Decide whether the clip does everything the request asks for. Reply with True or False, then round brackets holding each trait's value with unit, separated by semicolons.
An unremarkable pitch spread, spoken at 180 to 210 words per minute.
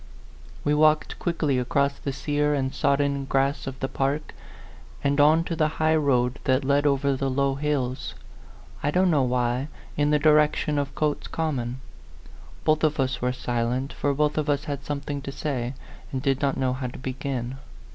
False (2.1 semitones; 185 wpm)